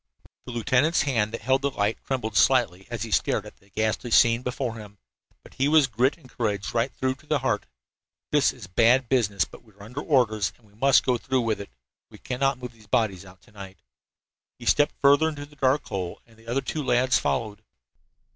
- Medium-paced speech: No, fast, 220 wpm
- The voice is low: Yes, low, 120 Hz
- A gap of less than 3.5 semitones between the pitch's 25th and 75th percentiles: No, average, 3.8 semitones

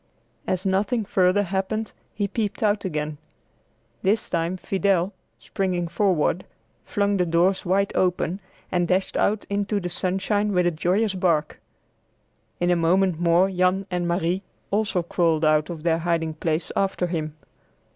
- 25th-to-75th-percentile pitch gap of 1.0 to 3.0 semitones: Yes, narrow, 2.6 semitones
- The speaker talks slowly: No, average, 145 wpm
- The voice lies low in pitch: No, medium, 185 Hz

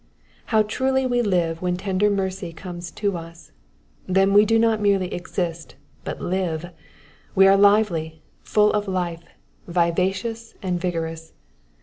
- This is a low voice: No, medium, 185 Hz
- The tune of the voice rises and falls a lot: No, average, 3.3 semitones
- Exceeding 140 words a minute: No, slow, 135 wpm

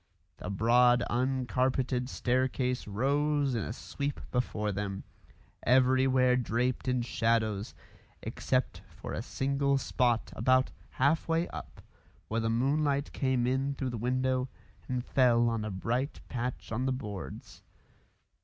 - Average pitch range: No, narrow, 2.2 semitones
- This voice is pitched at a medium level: No, low, 125 Hz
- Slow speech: Yes, slow, 130 wpm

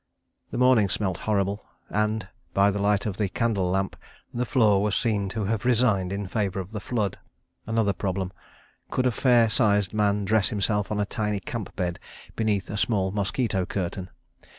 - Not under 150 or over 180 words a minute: Yes, average, 175 wpm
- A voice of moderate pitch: No, low, 105 Hz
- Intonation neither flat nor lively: No, narrow, 2.1 semitones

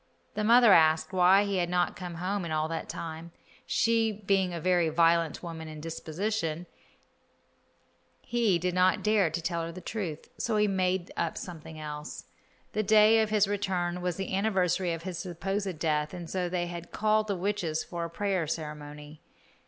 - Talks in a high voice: No, medium, 180 Hz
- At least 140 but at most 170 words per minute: No, average, 180 wpm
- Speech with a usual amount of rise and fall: Yes, average, 3.4 semitones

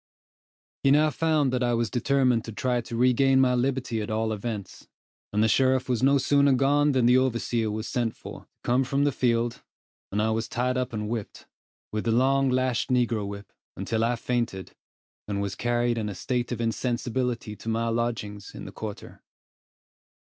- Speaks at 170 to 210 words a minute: Yes, average, 190 wpm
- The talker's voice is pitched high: No, low, 120 Hz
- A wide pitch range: No, narrow, 2.6 semitones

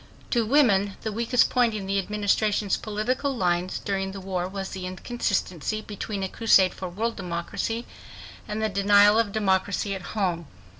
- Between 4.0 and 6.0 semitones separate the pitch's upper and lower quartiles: No, narrow, 2.5 semitones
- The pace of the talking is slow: No, average, 160 wpm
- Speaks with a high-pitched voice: Yes, high, 200 Hz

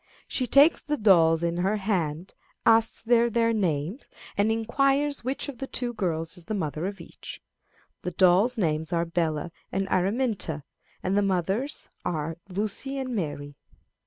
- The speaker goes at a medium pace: Yes, average, 155 wpm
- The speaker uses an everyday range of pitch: No, wide, 5.8 semitones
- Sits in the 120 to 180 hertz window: No, high, 195 Hz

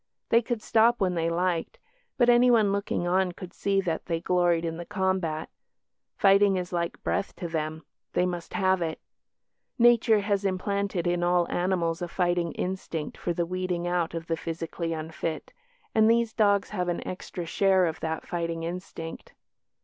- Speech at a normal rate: Yes, average, 170 wpm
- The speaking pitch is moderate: Yes, medium, 180 Hz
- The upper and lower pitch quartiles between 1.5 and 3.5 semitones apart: Yes, average, 2.8 semitones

